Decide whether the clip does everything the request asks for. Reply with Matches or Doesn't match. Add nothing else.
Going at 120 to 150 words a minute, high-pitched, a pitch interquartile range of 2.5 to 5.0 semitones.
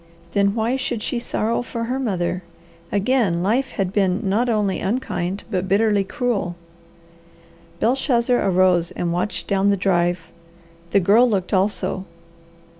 Matches